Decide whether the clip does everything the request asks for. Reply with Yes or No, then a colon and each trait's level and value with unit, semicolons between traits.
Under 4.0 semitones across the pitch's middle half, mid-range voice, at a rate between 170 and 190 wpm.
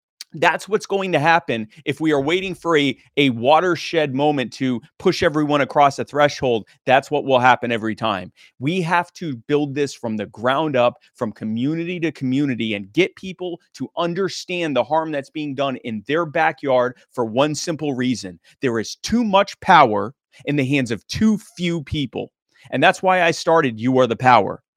No: average, 5.0 semitones; medium, 145 Hz; average, 185 wpm